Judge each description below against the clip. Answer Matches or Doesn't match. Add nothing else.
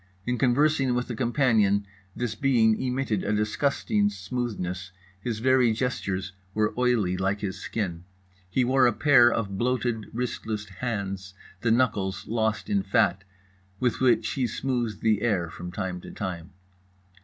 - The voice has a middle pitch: Doesn't match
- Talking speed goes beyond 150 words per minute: Doesn't match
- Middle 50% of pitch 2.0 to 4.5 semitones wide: Matches